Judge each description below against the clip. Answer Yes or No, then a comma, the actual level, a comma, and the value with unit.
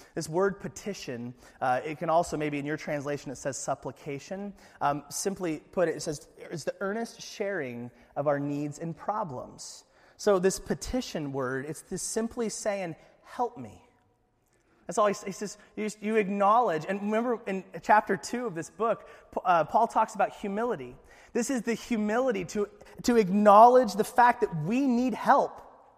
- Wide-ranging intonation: Yes, wide, 5.9 semitones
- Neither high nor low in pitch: No, high, 200 Hz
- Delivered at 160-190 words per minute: Yes, average, 170 wpm